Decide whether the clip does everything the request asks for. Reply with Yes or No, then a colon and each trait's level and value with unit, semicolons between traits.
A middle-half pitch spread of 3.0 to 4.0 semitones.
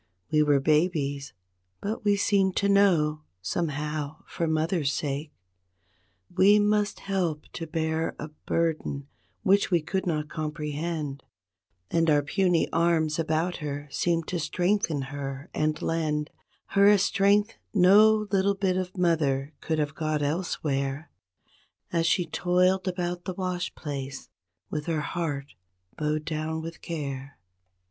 Yes: average, 3.5 semitones